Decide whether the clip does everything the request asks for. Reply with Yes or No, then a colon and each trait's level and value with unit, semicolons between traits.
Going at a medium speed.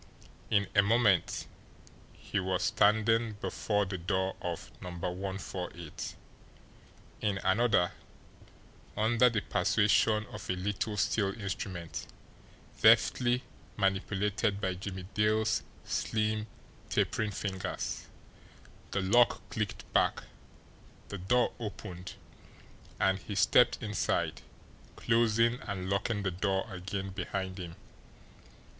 No: slow, 100 wpm